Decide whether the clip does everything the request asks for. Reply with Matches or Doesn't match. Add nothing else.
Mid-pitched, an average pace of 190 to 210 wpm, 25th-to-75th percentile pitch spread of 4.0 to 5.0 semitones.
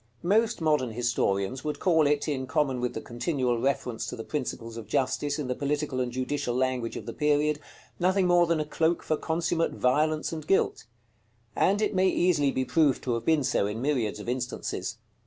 Matches